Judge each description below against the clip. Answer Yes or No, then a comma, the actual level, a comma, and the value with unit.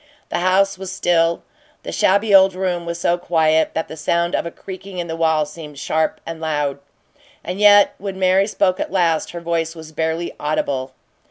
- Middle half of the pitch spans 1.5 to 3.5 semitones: Yes, average, 2.7 semitones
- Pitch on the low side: No, medium, 170 Hz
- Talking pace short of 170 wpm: No, average, 190 wpm